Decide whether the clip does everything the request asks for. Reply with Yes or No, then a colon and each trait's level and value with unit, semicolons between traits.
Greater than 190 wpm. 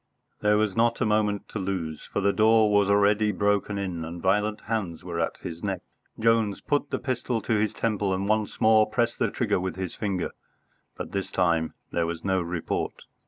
Yes: average, 200 wpm